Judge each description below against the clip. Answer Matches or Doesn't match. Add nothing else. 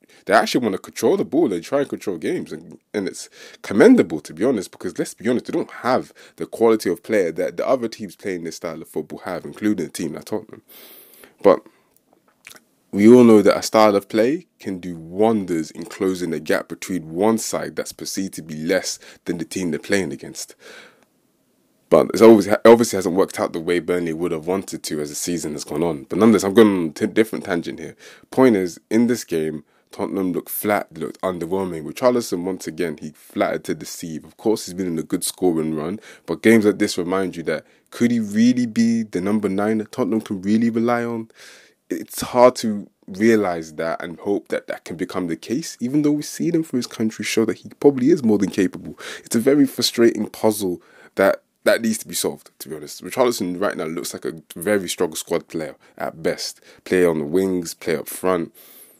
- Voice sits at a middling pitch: Doesn't match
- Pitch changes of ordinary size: Matches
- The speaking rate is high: Matches